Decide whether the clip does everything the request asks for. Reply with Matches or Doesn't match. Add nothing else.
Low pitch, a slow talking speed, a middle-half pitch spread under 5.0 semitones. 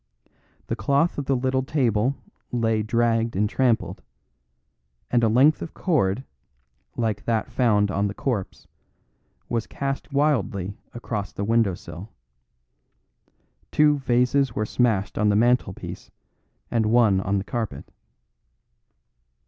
Matches